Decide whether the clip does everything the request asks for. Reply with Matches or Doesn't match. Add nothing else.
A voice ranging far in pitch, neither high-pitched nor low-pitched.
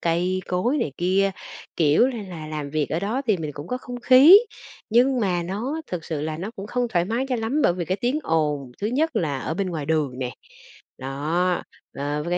Matches